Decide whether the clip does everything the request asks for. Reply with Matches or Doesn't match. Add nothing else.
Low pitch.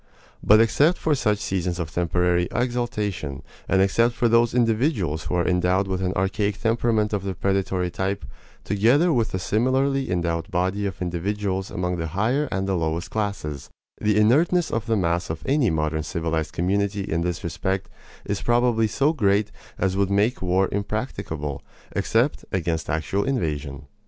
Matches